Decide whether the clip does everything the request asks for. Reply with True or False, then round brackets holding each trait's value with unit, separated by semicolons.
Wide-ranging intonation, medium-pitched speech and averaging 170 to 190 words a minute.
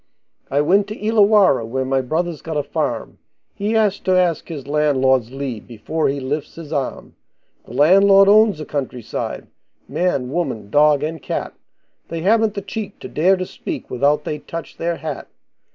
True (5.8 semitones; 155 Hz; 175 wpm)